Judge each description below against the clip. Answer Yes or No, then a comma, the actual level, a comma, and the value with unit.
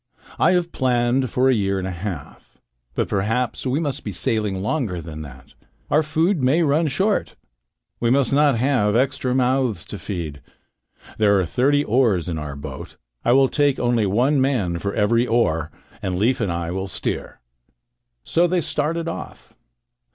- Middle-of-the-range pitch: No, low, 120 Hz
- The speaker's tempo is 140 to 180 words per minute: Yes, average, 165 wpm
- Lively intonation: Yes, wide, 6.4 semitones